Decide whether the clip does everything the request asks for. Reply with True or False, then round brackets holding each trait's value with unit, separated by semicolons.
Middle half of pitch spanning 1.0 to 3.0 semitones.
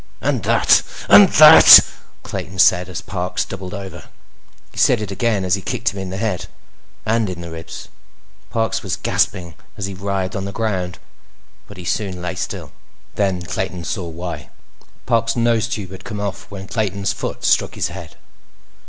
True (2.6 semitones)